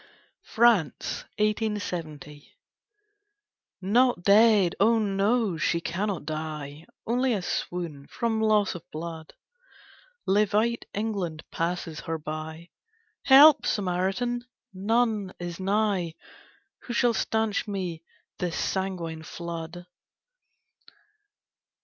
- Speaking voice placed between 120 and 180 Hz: No, high, 190 Hz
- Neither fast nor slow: No, slow, 90 wpm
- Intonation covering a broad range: No, average, 4.7 semitones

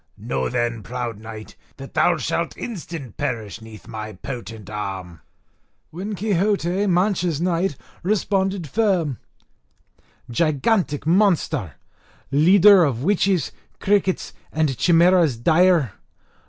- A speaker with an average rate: No, slow, 100 wpm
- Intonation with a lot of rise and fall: Yes, wide, 8.1 semitones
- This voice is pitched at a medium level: Yes, medium, 160 Hz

